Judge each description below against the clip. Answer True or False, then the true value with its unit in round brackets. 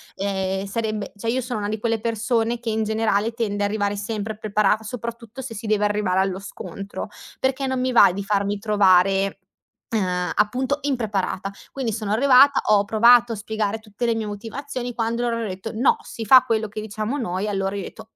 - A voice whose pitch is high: True (215 Hz)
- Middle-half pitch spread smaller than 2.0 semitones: False (2.5 semitones)